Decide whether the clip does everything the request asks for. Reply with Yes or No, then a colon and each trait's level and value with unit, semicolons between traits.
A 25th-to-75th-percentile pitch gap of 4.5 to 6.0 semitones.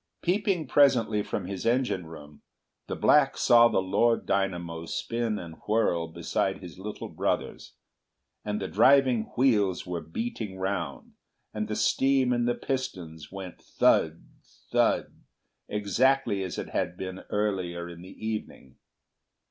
Yes: wide, 5.4 semitones